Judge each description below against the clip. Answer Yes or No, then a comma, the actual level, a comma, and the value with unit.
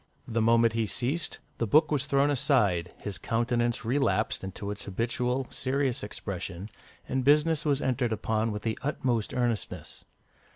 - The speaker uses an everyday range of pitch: Yes, average, 3.8 semitones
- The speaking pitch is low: Yes, low, 120 Hz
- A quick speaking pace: No, average, 150 wpm